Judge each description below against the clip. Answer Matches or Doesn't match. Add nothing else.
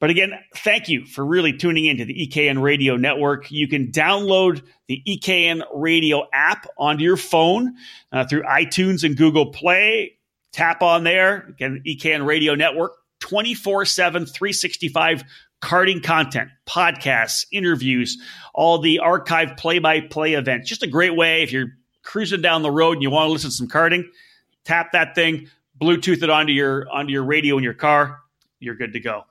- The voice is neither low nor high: Matches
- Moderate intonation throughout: Matches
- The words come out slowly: Doesn't match